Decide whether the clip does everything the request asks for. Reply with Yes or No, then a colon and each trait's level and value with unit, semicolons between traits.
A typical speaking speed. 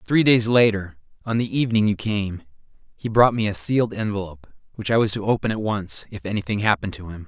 No: fast, 215 wpm